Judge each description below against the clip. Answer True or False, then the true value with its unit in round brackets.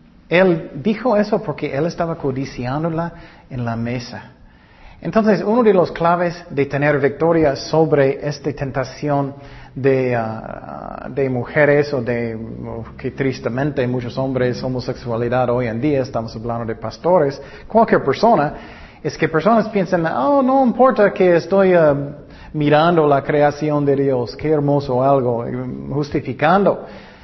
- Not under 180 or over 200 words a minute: False (135 wpm)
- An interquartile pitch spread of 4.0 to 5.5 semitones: True (4.7 semitones)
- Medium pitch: True (145 Hz)